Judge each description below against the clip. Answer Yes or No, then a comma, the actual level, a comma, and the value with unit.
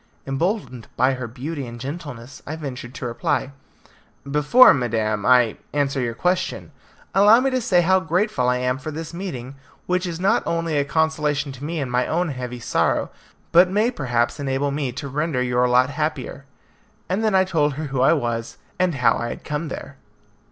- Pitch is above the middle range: No, medium, 145 Hz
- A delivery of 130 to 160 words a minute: No, average, 185 wpm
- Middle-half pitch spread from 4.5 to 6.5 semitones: Yes, average, 5.0 semitones